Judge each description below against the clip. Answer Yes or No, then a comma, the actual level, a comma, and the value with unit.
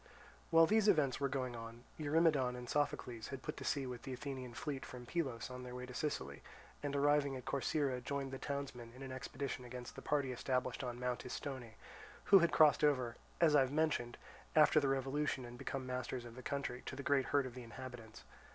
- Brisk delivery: Yes, fast, 210 wpm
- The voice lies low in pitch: Yes, low, 130 Hz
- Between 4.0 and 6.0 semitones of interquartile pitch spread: No, narrow, 2.5 semitones